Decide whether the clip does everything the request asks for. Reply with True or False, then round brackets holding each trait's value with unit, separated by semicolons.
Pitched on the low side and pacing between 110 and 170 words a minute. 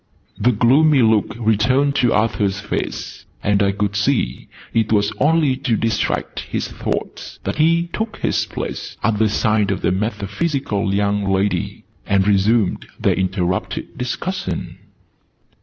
True (105 Hz; 140 wpm)